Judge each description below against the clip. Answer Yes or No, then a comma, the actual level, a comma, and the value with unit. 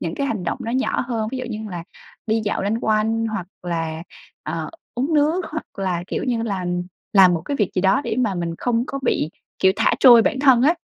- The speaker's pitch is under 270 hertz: Yes, high, 220 Hz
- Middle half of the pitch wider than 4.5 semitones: Yes, average, 5.2 semitones